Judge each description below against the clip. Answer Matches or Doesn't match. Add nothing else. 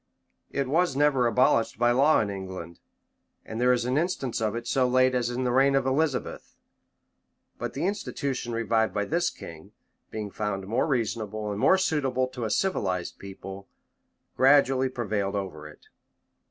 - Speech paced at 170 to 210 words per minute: Doesn't match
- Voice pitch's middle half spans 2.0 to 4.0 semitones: Doesn't match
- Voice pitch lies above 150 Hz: Doesn't match